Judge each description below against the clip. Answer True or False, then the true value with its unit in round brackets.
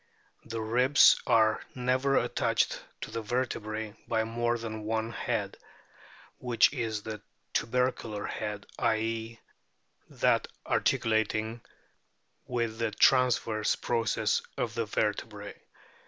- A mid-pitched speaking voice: False (115 Hz)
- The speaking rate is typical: False (105 wpm)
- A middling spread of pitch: False (1.6 semitones)